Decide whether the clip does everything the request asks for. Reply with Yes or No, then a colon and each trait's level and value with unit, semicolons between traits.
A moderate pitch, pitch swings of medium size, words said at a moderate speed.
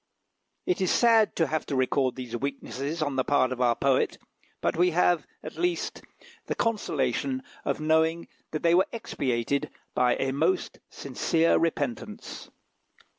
Yes: medium, 145 Hz; average, 4.6 semitones; average, 150 wpm